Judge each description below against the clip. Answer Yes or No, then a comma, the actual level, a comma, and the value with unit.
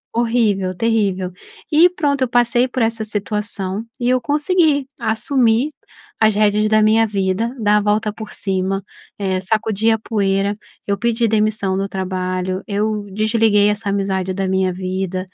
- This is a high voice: Yes, high, 210 Hz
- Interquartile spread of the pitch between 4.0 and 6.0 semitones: No, average, 2.9 semitones